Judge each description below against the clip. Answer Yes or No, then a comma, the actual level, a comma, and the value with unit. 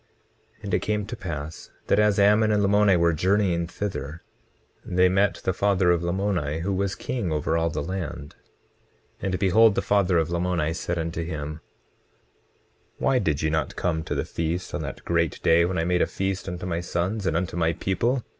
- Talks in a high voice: No, very low, 90 Hz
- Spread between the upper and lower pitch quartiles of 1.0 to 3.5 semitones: Yes, average, 3.2 semitones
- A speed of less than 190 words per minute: No, average, 200 wpm